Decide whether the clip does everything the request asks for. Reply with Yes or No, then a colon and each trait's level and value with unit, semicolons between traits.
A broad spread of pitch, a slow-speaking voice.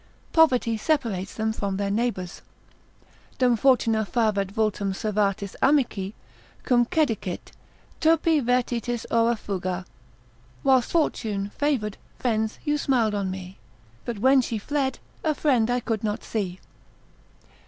No: average, 4.1 semitones; slow, 120 wpm